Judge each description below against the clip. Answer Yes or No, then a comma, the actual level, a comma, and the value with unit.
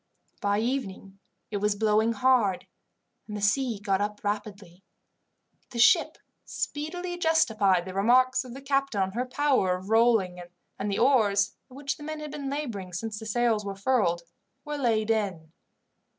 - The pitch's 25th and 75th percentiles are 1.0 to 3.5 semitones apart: No, average, 4.7 semitones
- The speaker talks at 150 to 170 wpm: Yes, average, 165 wpm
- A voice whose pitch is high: Yes, high, 220 Hz